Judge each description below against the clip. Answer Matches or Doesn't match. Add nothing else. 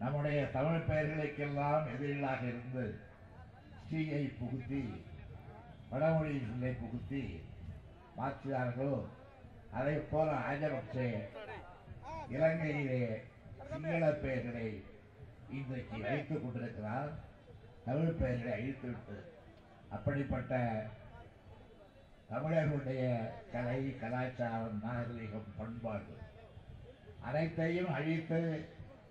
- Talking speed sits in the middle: Doesn't match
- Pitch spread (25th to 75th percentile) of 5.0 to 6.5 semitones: Doesn't match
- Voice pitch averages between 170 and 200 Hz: Doesn't match